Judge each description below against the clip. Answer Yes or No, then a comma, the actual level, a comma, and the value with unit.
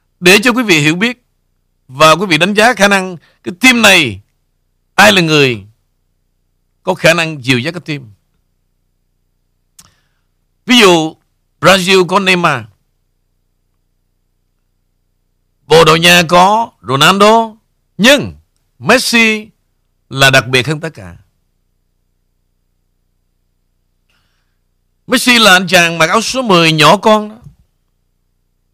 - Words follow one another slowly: Yes, slow, 115 wpm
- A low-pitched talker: Yes, low, 110 Hz